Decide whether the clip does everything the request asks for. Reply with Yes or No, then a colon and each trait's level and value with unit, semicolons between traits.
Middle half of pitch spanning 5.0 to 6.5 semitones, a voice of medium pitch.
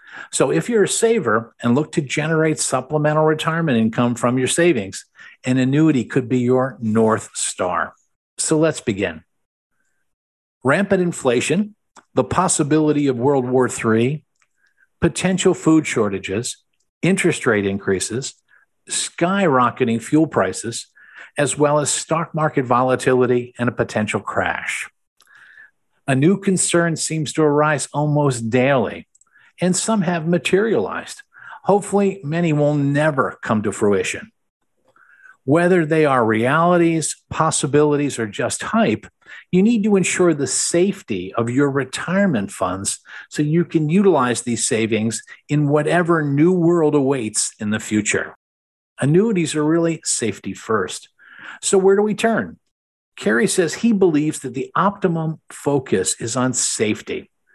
Yes: average, 5.3 semitones; medium, 150 Hz